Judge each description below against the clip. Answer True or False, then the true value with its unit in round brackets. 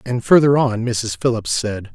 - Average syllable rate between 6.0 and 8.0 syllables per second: False (4.4 syllables/s)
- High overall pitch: False (120 Hz)